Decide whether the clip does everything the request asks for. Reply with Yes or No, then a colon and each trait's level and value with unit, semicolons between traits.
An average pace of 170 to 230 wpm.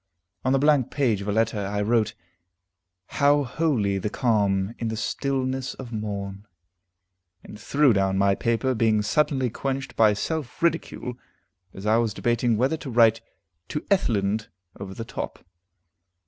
No: average, 150 wpm